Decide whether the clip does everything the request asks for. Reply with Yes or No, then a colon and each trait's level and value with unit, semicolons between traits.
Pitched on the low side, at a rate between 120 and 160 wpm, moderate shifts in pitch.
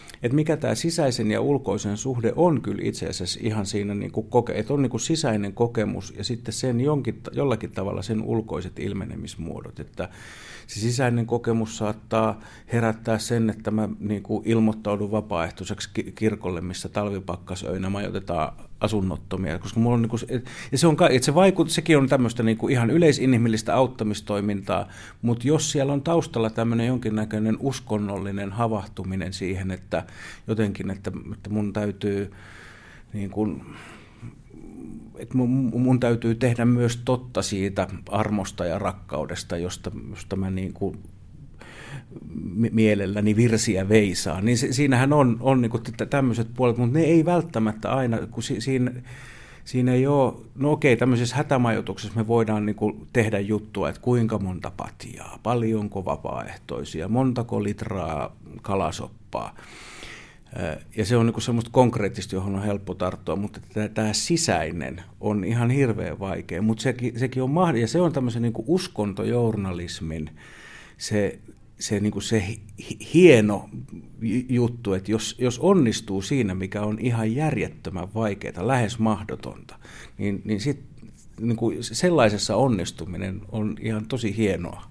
Yes: low, 110 Hz; average, 130 wpm; average, 3.3 semitones